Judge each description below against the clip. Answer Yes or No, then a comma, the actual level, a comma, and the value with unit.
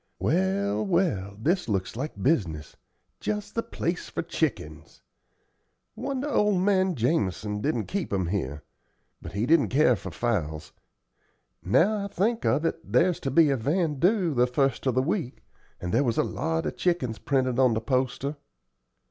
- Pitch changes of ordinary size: No, wide, 8.6 semitones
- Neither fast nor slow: Yes, average, 160 wpm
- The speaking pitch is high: No, low, 135 Hz